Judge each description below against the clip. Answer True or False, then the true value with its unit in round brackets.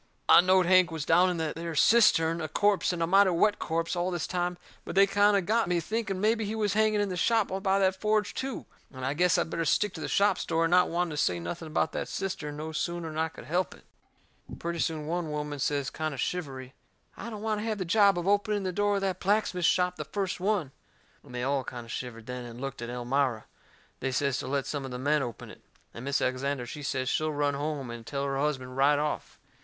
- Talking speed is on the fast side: True (250 wpm)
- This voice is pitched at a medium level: True (165 Hz)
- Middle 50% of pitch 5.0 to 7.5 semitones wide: True (5.5 semitones)